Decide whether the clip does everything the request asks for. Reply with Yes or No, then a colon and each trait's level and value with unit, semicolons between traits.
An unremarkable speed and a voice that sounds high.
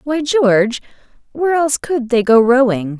Yes: average, 160 wpm; very high, 255 Hz